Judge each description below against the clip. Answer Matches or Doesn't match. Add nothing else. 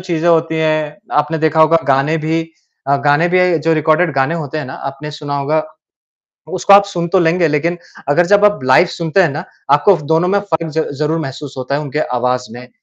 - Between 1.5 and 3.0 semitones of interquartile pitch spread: Matches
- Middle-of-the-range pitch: Matches